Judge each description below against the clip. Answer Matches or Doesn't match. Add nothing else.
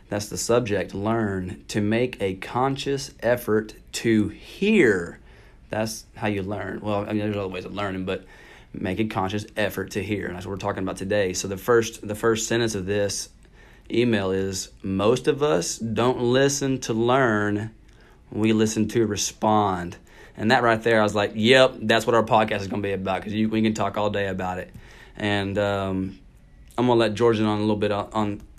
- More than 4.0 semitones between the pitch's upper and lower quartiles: Doesn't match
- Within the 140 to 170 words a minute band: Doesn't match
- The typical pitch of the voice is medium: Doesn't match